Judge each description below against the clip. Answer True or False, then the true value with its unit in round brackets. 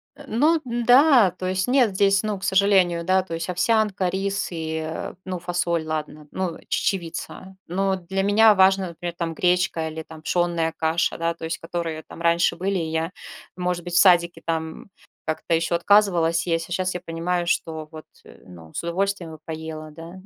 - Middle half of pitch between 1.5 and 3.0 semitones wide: True (2.7 semitones)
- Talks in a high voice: False (175 Hz)